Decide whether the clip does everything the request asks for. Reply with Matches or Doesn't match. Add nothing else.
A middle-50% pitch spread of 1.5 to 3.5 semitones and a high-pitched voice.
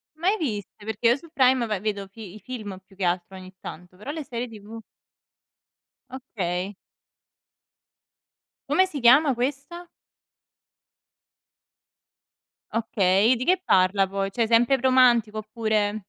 Doesn't match